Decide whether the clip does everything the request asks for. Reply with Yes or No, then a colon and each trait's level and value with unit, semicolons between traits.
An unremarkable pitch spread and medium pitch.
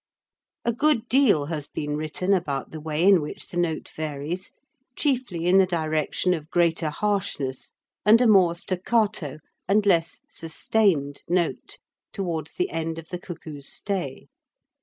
Yes: average, 4.3 semitones; medium, 170 Hz